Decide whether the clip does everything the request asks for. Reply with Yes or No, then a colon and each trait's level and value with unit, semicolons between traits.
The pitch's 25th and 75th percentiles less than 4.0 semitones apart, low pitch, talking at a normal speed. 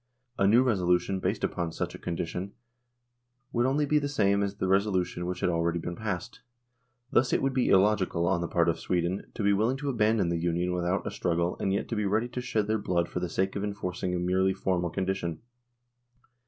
No: average, 3.5 semitones; very low, 95 Hz; fast, 215 wpm